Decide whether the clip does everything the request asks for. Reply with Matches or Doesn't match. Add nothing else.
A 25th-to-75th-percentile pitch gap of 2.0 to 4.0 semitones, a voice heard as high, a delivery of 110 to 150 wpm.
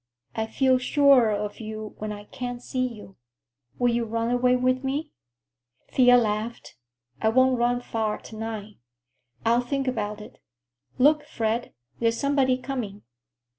Matches